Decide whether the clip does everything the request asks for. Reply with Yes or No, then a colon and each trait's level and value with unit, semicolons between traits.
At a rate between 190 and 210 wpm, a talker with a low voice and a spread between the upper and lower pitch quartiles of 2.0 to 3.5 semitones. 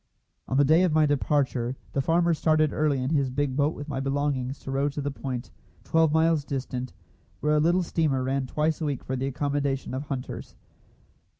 No: average, 200 wpm; medium, 145 Hz; narrow, 2.5 semitones